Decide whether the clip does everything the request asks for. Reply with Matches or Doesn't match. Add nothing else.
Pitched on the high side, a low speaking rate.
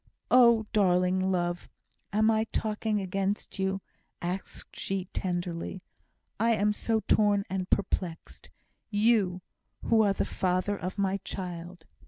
Matches